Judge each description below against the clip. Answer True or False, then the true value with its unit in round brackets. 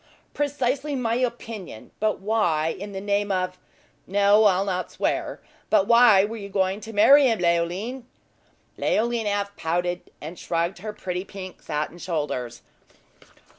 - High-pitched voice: True (200 Hz)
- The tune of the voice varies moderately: True (4.0 semitones)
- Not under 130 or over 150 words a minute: True (140 wpm)